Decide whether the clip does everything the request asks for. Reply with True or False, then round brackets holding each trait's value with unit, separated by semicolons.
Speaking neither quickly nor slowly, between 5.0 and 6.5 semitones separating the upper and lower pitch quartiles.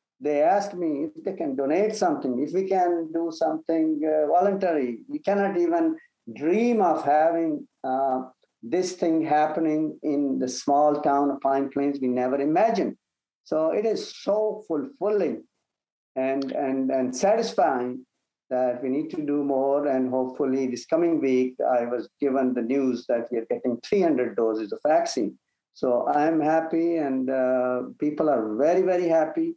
True (160 wpm; 5.4 semitones)